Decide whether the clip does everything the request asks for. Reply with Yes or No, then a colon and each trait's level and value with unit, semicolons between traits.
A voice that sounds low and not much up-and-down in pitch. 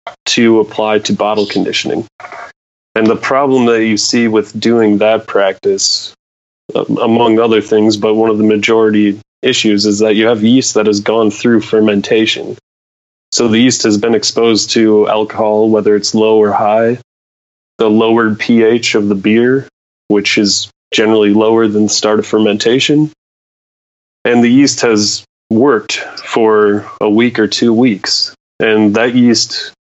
Yes: low, 110 Hz; narrow, 1.6 semitones